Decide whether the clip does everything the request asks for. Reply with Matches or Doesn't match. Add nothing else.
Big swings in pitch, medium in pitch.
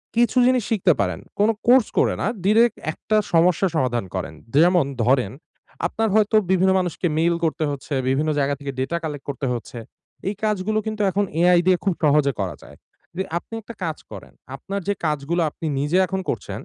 Matches